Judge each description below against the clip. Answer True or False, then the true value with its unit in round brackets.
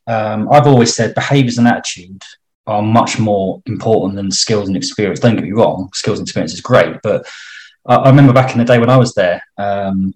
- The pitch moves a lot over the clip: False (3.8 semitones)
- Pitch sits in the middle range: False (115 Hz)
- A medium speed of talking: False (220 wpm)